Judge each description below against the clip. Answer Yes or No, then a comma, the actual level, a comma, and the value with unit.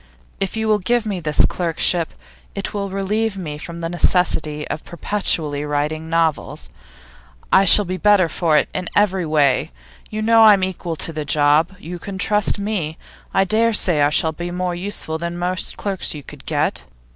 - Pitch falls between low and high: Yes, medium, 175 Hz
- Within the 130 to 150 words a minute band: No, average, 190 wpm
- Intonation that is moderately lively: Yes, average, 3.9 semitones